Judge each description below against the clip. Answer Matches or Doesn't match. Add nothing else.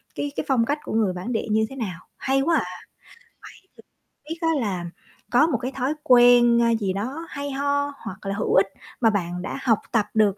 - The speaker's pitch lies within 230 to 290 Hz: Matches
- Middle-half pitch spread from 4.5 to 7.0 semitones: Matches